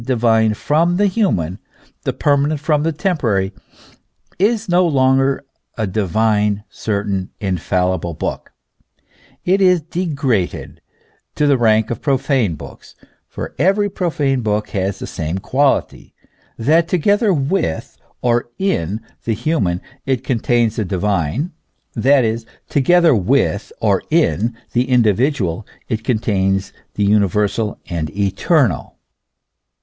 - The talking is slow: Yes, slow, 125 wpm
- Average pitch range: No, wide, 6.7 semitones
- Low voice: Yes, low, 120 Hz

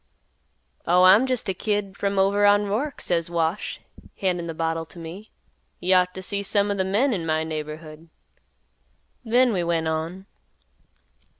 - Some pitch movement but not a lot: Yes, average, 3.7 semitones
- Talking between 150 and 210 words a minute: Yes, average, 165 wpm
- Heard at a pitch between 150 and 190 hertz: Yes, medium, 185 Hz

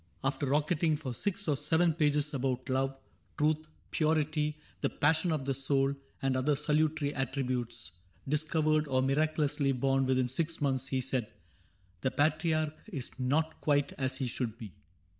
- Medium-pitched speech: Yes, medium, 145 Hz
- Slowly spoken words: No, average, 155 wpm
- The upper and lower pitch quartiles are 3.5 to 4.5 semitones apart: No, average, 2.8 semitones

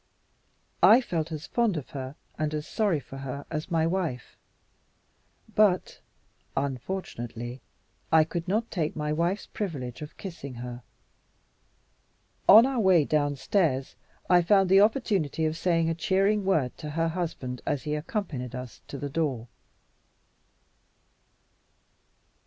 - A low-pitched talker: No, medium, 160 Hz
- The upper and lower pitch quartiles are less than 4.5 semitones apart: No, wide, 5.5 semitones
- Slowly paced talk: Yes, slow, 130 wpm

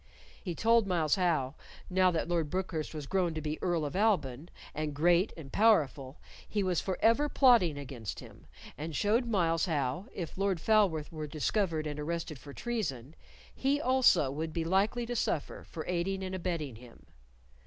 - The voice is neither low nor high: Yes, medium, 170 Hz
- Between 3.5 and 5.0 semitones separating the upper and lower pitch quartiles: Yes, average, 4.5 semitones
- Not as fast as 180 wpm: Yes, average, 170 wpm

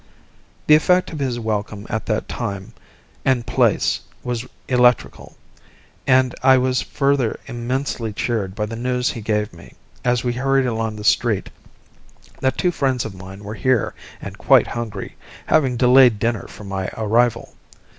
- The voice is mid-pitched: No, low, 120 Hz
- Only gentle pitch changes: No, average, 3.1 semitones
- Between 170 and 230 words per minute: No, average, 155 wpm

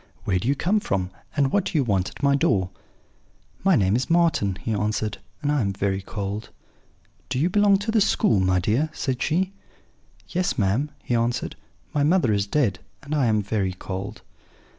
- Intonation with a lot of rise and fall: Yes, wide, 7.6 semitones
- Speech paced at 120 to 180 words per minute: No, average, 190 wpm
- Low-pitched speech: Yes, low, 120 Hz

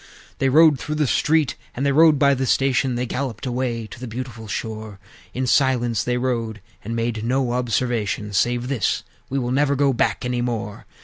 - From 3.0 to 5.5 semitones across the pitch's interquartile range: No, narrow, 2.6 semitones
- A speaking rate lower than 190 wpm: No, average, 195 wpm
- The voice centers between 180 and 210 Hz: No, low, 125 Hz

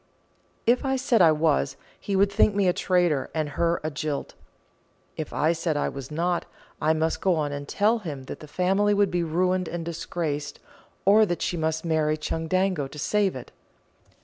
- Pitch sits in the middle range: Yes, medium, 170 Hz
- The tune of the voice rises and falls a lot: No, average, 3.8 semitones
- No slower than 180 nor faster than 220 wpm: Yes, average, 190 wpm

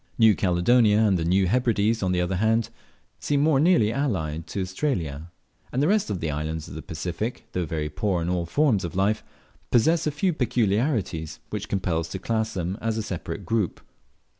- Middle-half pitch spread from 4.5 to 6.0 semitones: Yes, average, 5.2 semitones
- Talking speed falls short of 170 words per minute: No, average, 195 wpm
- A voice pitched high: No, low, 100 Hz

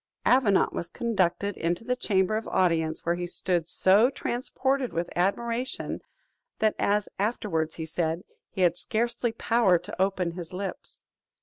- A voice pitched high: Yes, high, 195 Hz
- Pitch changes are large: No, average, 4.9 semitones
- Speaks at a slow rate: No, average, 145 wpm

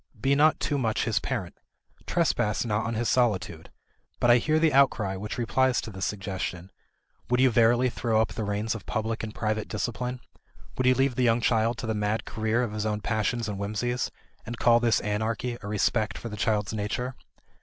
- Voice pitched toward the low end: Yes, low, 115 Hz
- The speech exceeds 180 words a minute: Yes, average, 200 wpm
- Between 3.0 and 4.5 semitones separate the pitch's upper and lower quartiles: No, narrow, 2.6 semitones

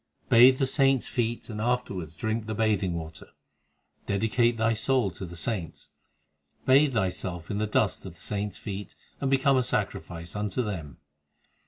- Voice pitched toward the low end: Yes, low, 110 Hz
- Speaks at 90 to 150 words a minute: No, average, 165 wpm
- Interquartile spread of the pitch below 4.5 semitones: No, average, 4.8 semitones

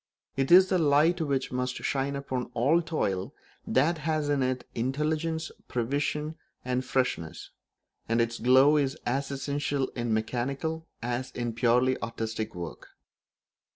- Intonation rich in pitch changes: No, average, 3.7 semitones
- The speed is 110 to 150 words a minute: Yes, slow, 135 wpm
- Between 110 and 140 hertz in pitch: Yes, low, 135 Hz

